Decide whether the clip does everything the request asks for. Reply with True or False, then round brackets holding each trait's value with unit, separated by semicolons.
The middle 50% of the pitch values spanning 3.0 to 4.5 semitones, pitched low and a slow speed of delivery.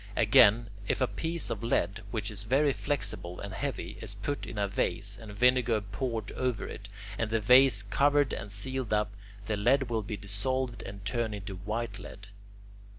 False (3.9 semitones; 110 Hz; 180 wpm)